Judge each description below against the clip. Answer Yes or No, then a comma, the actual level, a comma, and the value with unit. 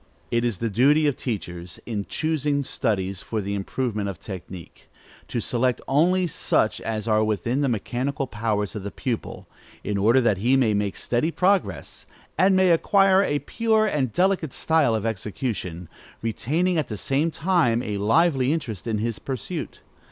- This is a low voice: Yes, low, 120 Hz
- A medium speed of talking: Yes, average, 165 wpm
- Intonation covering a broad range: Yes, wide, 6.5 semitones